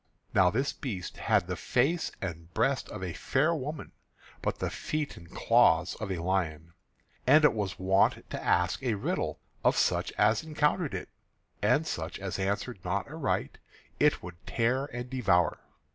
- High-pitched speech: No, low, 105 Hz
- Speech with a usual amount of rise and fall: No, wide, 6.9 semitones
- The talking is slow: No, average, 165 wpm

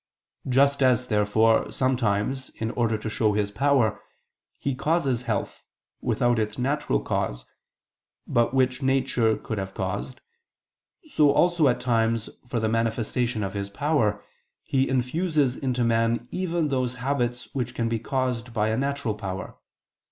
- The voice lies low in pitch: Yes, low, 120 Hz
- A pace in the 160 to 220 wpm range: No, average, 145 wpm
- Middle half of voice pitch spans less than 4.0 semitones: Yes, average, 3.3 semitones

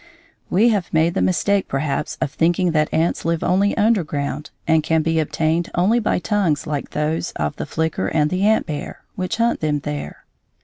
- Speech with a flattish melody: No, average, 3.7 semitones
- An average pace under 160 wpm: No, average, 185 wpm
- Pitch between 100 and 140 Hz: No, medium, 165 Hz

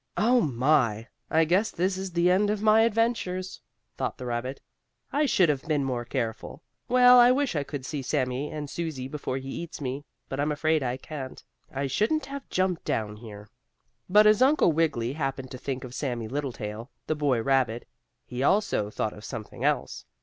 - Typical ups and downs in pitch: No, wide, 6.6 semitones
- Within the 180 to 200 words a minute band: Yes, average, 185 wpm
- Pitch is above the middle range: No, medium, 145 Hz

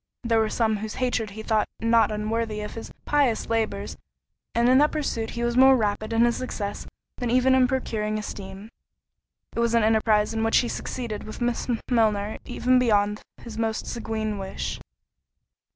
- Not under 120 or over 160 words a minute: No, average, 175 wpm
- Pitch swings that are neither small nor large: No, narrow, 1.9 semitones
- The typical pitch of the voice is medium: No, high, 225 Hz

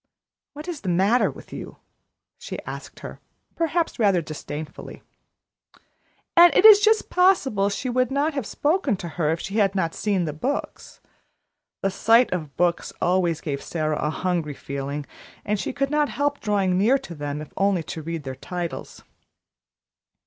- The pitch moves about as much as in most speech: No, wide, 9.0 semitones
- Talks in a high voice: Yes, high, 195 Hz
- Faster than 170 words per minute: No, average, 165 wpm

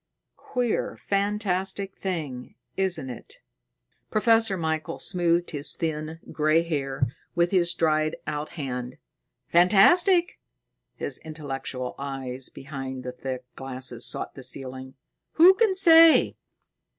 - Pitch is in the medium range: Yes, medium, 155 Hz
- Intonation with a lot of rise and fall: Yes, wide, 6.3 semitones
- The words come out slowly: Yes, slow, 110 wpm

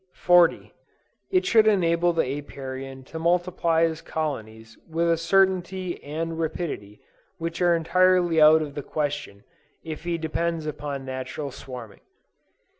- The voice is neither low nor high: Yes, medium, 160 Hz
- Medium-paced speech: No, slow, 130 wpm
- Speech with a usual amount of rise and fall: Yes, average, 3.4 semitones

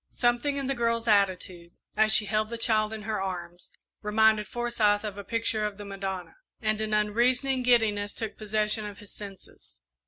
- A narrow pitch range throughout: Yes, narrow, 2.1 semitones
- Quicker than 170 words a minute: Yes, average, 180 wpm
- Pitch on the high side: Yes, high, 215 Hz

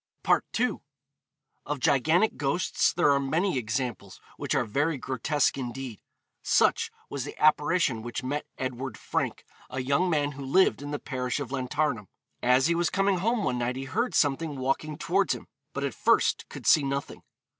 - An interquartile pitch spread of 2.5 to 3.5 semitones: Yes, average, 3.2 semitones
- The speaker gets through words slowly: No, average, 170 wpm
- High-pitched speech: No, medium, 140 Hz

